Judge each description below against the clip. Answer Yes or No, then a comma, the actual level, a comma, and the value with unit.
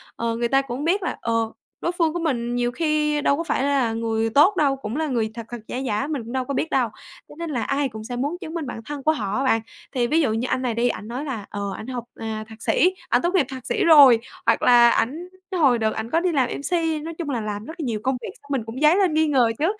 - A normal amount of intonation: Yes, average, 4.9 semitones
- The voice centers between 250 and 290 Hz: Yes, very high, 265 Hz